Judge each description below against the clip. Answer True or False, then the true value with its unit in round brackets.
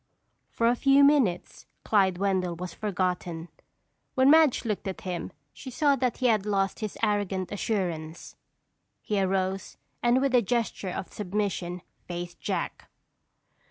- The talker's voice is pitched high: True (200 Hz)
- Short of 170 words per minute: True (140 wpm)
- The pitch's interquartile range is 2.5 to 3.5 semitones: False (4.7 semitones)